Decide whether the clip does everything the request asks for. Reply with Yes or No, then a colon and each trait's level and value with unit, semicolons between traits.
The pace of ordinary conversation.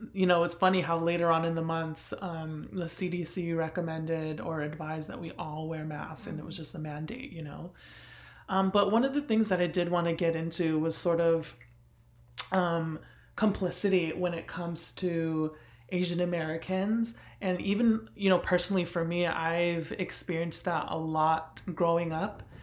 Yes: average, 180 wpm